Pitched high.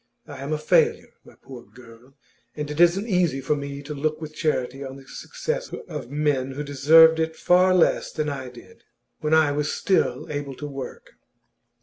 No: medium, 150 Hz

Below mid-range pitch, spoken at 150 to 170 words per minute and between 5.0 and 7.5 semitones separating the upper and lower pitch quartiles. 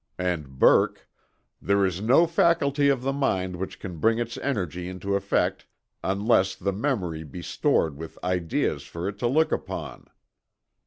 Yes: low, 100 Hz; average, 155 wpm; wide, 5.6 semitones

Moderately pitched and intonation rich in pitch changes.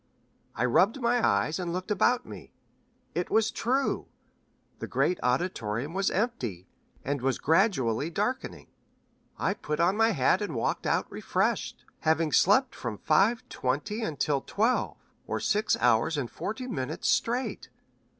Yes: medium, 175 Hz; wide, 8.9 semitones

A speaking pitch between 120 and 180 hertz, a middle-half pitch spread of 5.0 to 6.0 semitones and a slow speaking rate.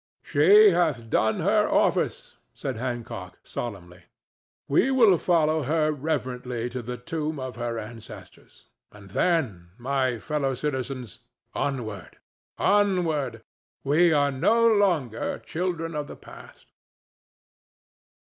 Yes: medium, 140 Hz; wide, 5.5 semitones; slow, 110 wpm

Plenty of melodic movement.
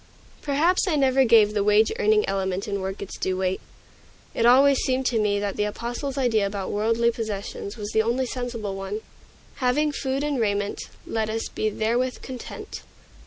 No: average, 4.2 semitones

